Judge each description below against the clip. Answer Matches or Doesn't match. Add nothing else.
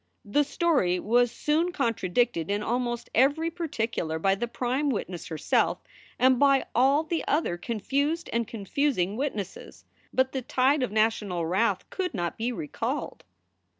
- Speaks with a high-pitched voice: Matches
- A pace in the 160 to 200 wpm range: Doesn't match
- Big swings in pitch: Matches